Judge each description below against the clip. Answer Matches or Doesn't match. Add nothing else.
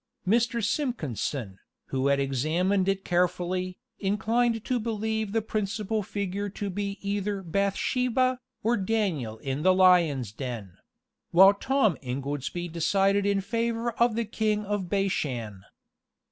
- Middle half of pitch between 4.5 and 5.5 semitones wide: Matches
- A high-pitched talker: Matches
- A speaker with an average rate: Doesn't match